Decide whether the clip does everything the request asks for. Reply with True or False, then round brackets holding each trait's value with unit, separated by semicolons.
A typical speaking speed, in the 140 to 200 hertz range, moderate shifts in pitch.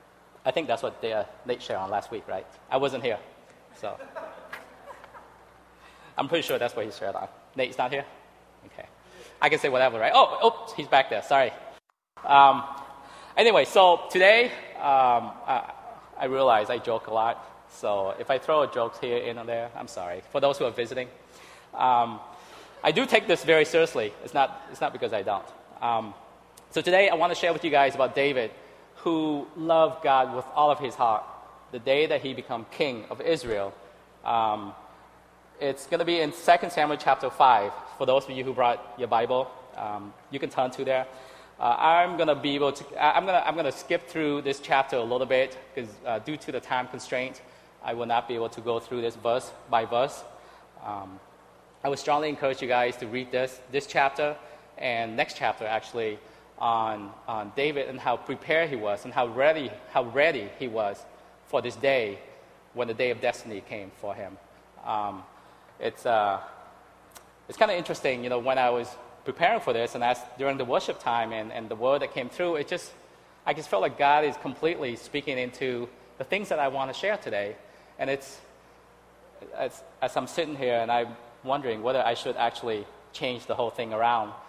False (195 wpm; 130 Hz; 3.9 semitones)